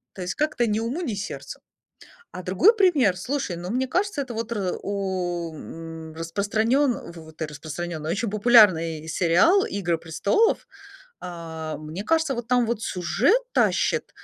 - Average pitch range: No, wide, 6.8 semitones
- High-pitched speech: Yes, high, 200 Hz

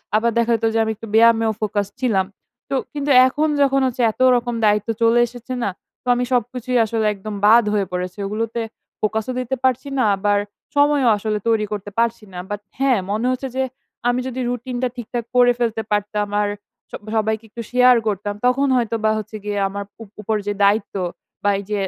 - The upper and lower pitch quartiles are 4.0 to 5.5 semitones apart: No, average, 3.0 semitones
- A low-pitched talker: No, high, 225 Hz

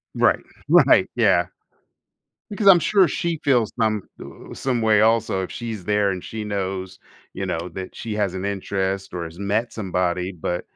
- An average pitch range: Yes, average, 3.3 semitones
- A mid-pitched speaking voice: No, low, 100 Hz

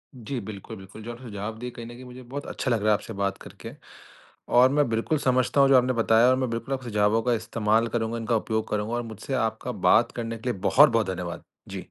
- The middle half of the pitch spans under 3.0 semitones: Yes, narrow, 2.6 semitones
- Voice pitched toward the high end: No, low, 115 Hz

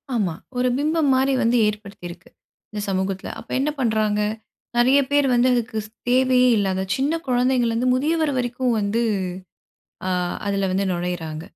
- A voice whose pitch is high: Yes, high, 235 Hz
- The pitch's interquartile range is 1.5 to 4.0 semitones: No, average, 4.7 semitones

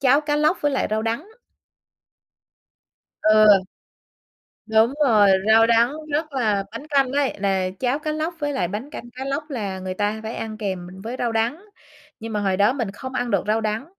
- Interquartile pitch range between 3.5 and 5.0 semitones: Yes, average, 4.6 semitones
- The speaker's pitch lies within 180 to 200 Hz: No, high, 230 Hz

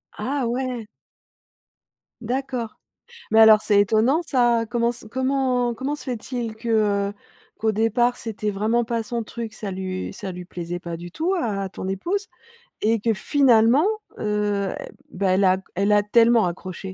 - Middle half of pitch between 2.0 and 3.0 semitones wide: No, average, 3.4 semitones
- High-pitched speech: Yes, high, 225 Hz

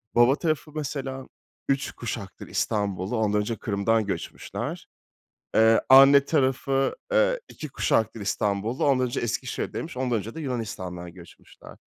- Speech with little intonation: No, average, 4.6 semitones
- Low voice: Yes, low, 120 Hz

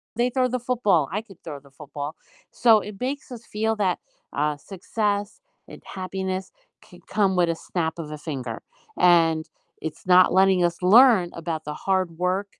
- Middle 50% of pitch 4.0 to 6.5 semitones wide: Yes, average, 4.4 semitones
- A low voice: No, medium, 185 Hz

